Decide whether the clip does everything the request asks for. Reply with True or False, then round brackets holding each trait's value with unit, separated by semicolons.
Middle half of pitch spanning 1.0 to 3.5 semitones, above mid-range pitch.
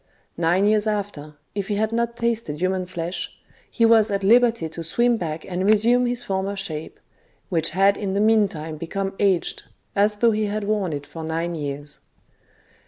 False (4.6 semitones; 195 Hz)